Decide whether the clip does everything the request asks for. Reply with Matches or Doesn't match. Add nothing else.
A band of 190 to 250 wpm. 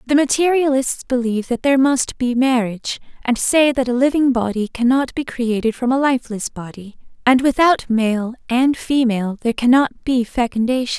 Doesn't match